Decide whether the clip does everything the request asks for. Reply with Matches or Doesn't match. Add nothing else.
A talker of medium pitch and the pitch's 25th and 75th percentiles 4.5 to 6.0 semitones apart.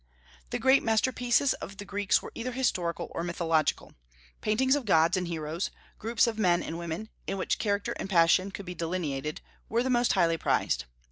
Doesn't match